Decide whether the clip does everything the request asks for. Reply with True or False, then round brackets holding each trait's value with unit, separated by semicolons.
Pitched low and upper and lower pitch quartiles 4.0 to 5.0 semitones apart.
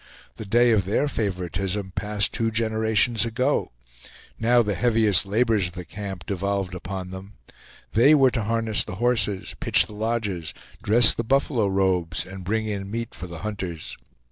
False (105 Hz; 3.1 semitones)